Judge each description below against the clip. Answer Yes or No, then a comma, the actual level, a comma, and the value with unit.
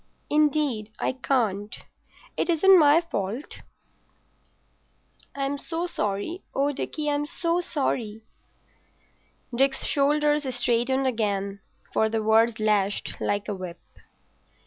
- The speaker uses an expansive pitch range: Yes, wide, 5.7 semitones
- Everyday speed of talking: No, slow, 105 wpm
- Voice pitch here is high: Yes, very high, 260 Hz